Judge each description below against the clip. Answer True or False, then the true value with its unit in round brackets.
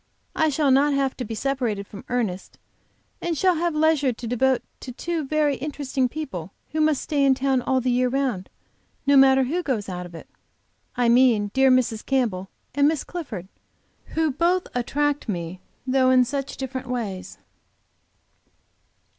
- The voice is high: True (265 Hz)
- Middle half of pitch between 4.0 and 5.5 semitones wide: False (3.5 semitones)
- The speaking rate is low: False (165 wpm)